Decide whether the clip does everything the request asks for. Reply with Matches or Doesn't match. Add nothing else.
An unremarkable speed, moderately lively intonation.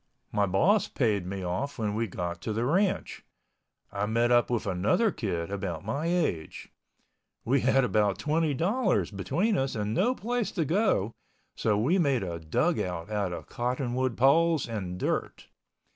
Doesn't match